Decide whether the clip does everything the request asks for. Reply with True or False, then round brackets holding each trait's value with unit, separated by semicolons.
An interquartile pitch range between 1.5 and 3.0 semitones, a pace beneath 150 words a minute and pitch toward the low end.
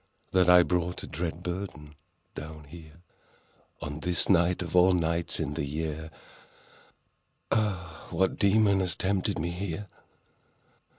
True (2.6 semitones; 135 wpm; 85 Hz)